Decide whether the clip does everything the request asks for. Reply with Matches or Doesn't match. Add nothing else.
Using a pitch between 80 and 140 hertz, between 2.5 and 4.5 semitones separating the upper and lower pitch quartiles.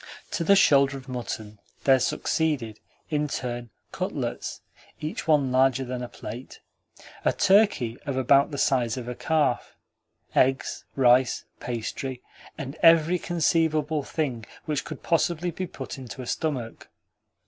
Matches